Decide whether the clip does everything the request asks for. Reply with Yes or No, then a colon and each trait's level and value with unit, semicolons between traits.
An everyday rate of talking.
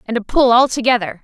No: fast, 240 wpm